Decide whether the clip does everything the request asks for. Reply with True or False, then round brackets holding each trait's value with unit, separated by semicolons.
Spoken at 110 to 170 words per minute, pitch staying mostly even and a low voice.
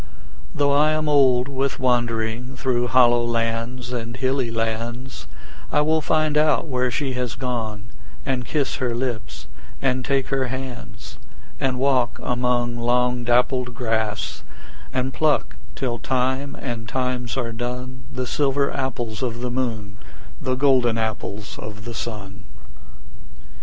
True (135 wpm; 2.1 semitones; 125 Hz)